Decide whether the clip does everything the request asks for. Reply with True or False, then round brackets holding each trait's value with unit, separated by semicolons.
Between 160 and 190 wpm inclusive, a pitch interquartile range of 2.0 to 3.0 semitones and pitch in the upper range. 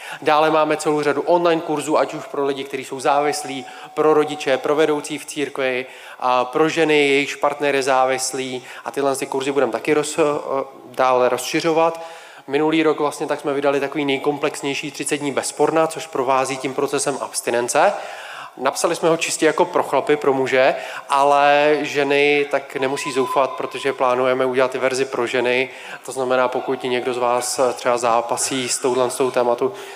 False (170 wpm; 2.5 semitones; 140 Hz)